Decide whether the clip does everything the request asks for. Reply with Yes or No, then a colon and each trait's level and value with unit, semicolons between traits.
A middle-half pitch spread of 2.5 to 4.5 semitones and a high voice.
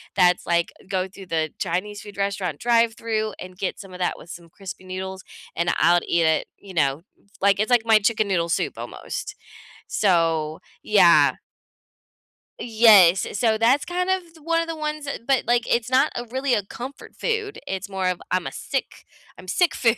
No: average, 5.0 semitones; high, 200 Hz